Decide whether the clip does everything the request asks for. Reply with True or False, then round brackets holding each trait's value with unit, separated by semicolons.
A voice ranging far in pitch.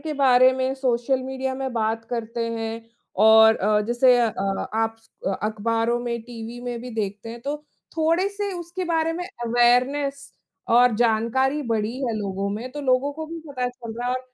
False (3.1 semitones)